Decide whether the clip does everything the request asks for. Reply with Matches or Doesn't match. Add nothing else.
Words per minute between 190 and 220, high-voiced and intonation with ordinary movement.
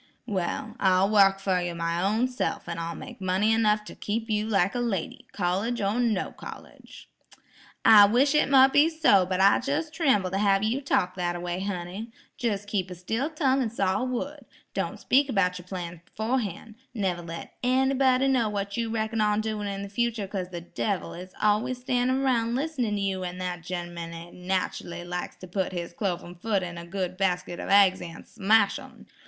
Matches